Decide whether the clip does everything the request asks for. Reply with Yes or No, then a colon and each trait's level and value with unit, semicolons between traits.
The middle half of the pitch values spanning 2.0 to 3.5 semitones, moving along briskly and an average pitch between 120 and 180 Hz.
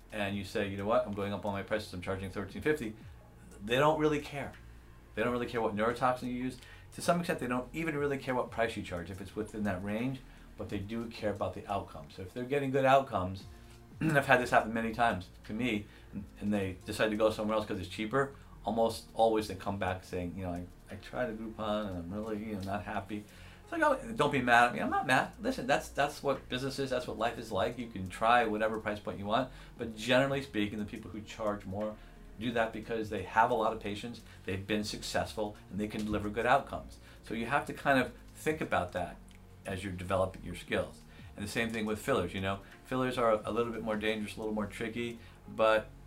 No: average, 3.2 semitones; fast, 240 wpm; low, 110 Hz